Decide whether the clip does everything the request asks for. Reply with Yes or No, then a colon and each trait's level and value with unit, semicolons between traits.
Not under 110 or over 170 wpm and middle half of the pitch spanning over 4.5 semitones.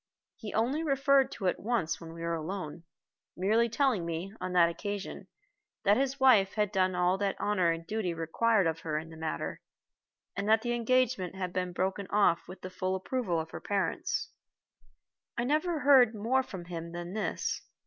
No: average, 185 wpm; average, 5.1 semitones